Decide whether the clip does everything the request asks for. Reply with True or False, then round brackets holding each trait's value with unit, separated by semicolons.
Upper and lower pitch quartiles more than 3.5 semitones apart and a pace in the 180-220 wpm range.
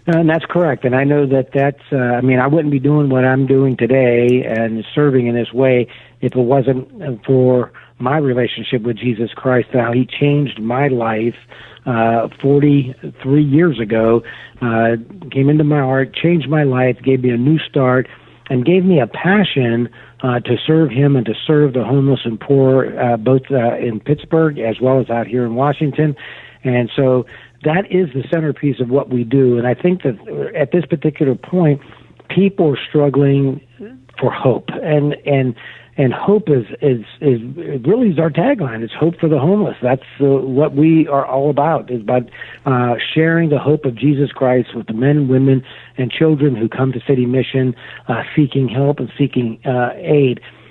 False (3.0 semitones; 190 wpm)